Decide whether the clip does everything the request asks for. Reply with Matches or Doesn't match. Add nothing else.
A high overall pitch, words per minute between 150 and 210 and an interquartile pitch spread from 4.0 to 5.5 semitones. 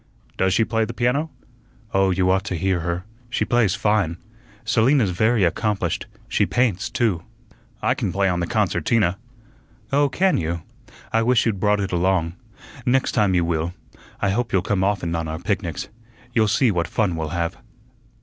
Doesn't match